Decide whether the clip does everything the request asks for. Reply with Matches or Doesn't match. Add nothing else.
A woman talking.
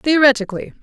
Matches